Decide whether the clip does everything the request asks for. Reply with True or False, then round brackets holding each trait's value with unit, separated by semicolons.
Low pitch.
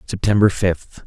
True (95 Hz)